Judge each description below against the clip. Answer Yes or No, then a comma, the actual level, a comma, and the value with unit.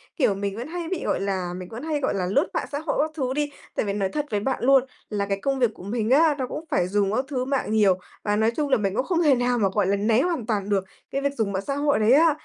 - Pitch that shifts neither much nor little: No, wide, 6.0 semitones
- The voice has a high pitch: Yes, high, 240 Hz